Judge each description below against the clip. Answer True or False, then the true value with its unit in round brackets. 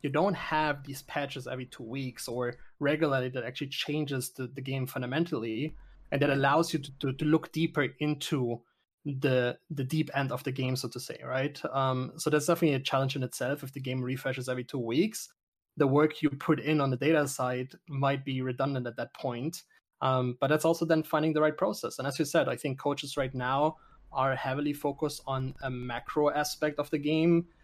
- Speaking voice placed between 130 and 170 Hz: True (140 Hz)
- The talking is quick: True (210 wpm)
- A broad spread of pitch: False (2.7 semitones)